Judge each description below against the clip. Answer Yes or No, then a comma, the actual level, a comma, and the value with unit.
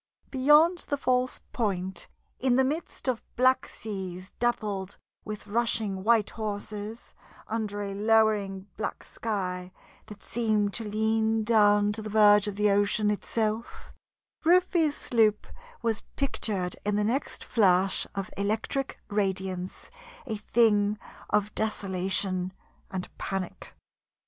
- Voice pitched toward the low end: No, high, 210 Hz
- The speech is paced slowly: Yes, slow, 120 wpm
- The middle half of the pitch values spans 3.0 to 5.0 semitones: No, narrow, 2.4 semitones